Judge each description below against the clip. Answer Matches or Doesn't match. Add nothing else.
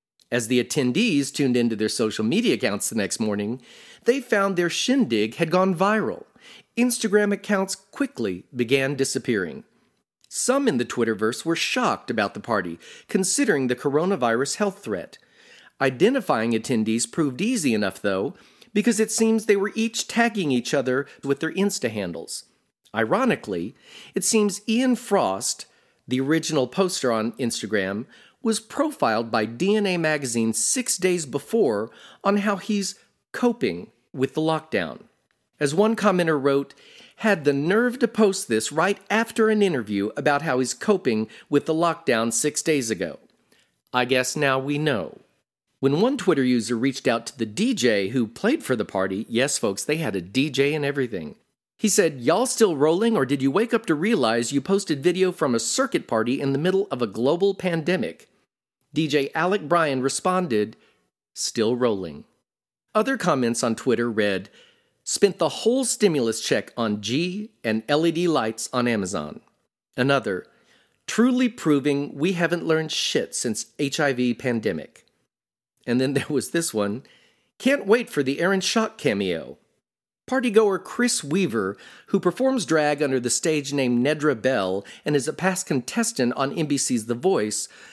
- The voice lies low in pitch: Doesn't match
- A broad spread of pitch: Matches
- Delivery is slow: Doesn't match